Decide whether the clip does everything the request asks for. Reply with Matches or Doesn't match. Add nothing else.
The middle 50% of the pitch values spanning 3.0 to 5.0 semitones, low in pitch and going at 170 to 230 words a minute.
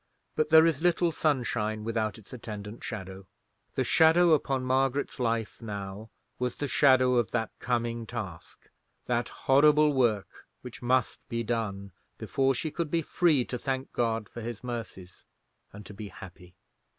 Doesn't match